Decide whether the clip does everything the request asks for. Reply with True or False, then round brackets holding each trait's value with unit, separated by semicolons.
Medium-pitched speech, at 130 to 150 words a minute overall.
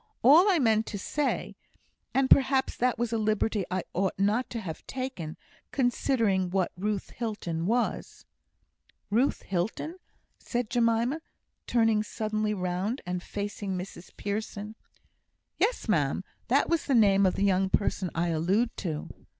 False (215 Hz; 145 wpm)